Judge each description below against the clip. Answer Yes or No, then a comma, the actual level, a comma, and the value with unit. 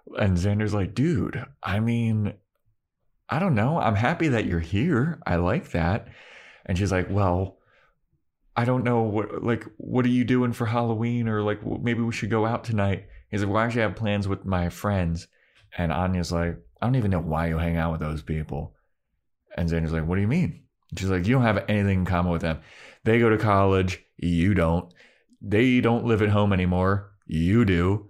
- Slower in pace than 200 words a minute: No, fast, 205 wpm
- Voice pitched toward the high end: No, low, 100 Hz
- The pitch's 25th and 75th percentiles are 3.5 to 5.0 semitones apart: Yes, average, 4.7 semitones